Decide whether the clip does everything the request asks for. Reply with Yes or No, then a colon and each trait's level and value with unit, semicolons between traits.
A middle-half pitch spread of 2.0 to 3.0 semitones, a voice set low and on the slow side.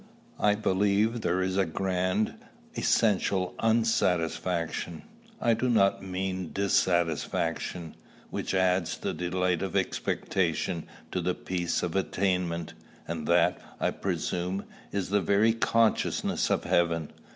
Yes: narrow, 2.5 semitones; very low, 95 Hz; slow, 120 wpm